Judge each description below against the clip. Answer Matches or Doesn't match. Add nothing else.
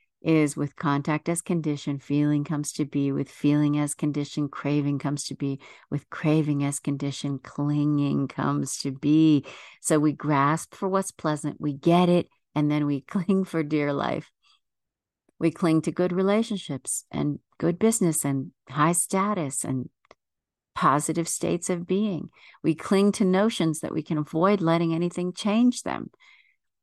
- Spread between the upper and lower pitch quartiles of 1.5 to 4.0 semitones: Matches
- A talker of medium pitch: Matches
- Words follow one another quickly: Doesn't match